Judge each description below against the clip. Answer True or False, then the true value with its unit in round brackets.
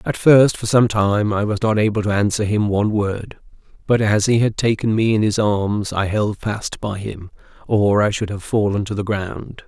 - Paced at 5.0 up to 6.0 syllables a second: False (4.7 syllables/s)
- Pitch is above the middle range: False (105 Hz)